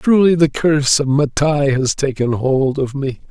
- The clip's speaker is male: Yes, male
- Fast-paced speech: No, average, 180 wpm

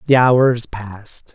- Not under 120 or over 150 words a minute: Yes, slow, 135 wpm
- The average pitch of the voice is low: Yes, low, 120 Hz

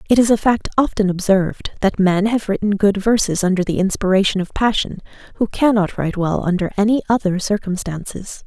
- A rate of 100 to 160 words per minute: No, average, 175 wpm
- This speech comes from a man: No, female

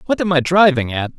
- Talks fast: Yes, fast, 255 wpm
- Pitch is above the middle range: No, medium, 155 Hz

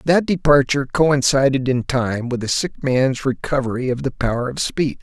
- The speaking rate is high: No, average, 180 wpm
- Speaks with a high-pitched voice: No, low, 135 Hz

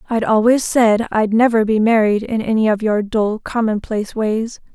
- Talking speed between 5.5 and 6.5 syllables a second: No, 4.8 syllables/s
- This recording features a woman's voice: Yes, female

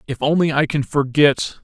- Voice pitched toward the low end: No, medium, 145 Hz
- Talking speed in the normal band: Yes, average, 185 wpm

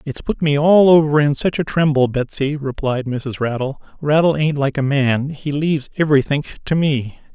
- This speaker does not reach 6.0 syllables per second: Yes, 5.0 syllables/s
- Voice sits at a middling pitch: Yes, medium, 145 Hz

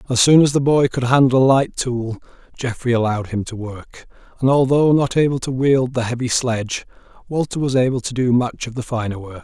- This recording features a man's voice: Yes, male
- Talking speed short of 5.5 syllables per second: No, 5.6 syllables/s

